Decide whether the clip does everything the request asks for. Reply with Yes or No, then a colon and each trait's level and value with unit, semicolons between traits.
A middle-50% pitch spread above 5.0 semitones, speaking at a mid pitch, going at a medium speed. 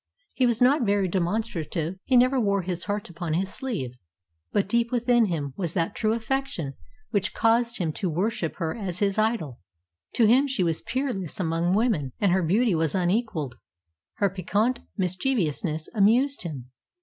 No: wide, 5.6 semitones; high, 200 Hz; average, 165 wpm